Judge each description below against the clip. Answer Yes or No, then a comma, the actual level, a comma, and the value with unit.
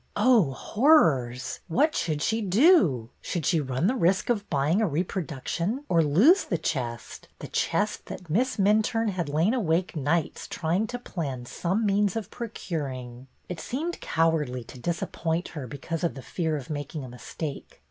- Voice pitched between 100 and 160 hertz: No, medium, 170 Hz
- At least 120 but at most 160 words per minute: No, average, 170 wpm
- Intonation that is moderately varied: No, wide, 6.6 semitones